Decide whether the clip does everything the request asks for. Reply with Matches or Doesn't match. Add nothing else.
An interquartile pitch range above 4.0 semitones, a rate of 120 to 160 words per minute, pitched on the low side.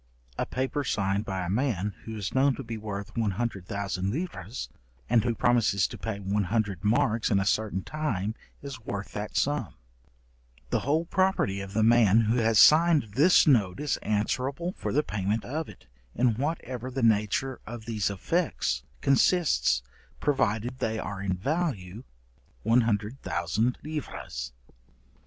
Matches